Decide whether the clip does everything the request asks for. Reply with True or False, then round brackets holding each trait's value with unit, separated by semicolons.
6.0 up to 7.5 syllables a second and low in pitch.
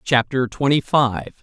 False (3.9 syllables/s; 130 Hz)